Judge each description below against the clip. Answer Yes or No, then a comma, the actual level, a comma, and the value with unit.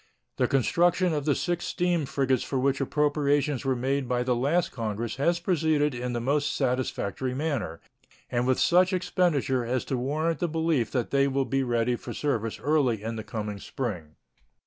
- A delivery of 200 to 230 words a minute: No, average, 180 wpm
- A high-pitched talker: No, low, 135 Hz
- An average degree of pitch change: Yes, average, 4.0 semitones